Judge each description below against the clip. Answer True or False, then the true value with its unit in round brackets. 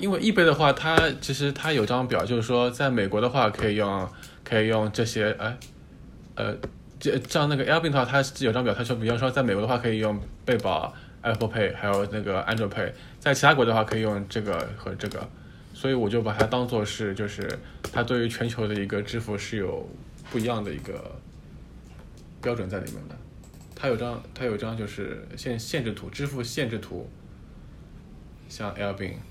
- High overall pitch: False (110 Hz)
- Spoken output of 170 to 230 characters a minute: False (315 characters per minute)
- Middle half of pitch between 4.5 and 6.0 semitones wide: False (3.4 semitones)